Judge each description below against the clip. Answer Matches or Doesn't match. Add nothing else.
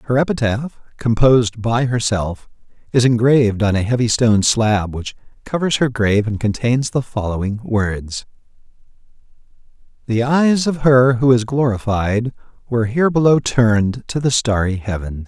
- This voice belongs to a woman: Doesn't match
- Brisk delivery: Doesn't match